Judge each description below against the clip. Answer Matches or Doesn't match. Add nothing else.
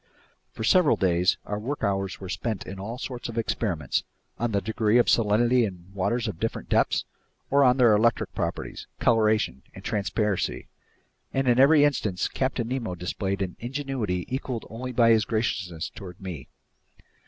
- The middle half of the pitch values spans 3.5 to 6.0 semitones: Matches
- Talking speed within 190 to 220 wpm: Doesn't match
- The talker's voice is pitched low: Matches